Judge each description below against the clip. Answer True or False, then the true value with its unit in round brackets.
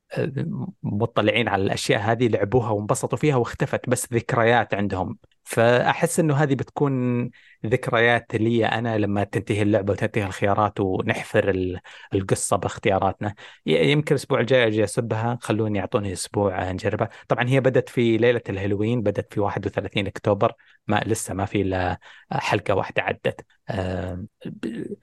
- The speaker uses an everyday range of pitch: True (3.3 semitones)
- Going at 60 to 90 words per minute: False (130 wpm)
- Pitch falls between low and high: False (110 Hz)